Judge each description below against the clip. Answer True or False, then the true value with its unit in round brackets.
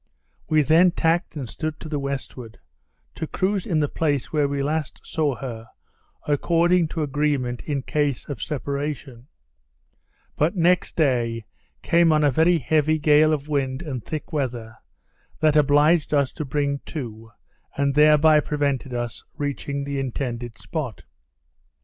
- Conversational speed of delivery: True (145 wpm)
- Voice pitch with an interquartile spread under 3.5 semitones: True (2.8 semitones)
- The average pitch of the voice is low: False (145 Hz)